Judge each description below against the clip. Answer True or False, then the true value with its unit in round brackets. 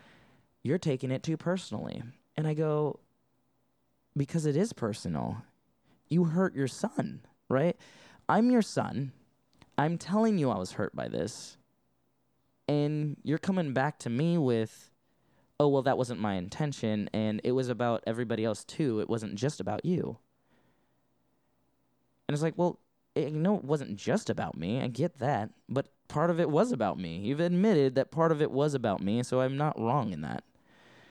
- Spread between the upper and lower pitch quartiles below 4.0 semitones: False (5.4 semitones)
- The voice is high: False (140 Hz)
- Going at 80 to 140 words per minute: False (175 wpm)